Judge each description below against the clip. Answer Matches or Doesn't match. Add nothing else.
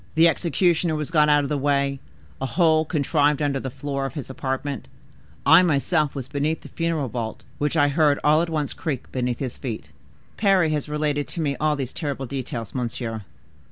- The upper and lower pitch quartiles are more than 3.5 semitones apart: Doesn't match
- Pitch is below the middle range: Doesn't match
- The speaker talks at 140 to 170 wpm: Doesn't match